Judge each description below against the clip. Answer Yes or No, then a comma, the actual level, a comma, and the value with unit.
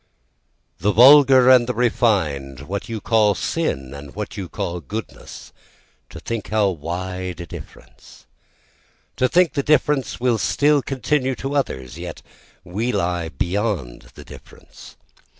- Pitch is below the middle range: Yes, low, 105 Hz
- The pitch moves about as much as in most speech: No, wide, 6.7 semitones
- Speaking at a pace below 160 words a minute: Yes, slow, 135 wpm